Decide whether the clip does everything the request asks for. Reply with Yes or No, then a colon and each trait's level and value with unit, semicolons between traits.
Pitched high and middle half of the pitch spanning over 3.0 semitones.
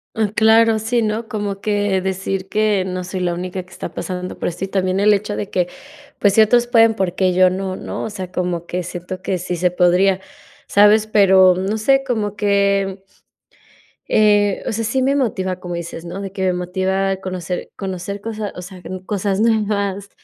No: high, 195 Hz; narrow, 2.4 semitones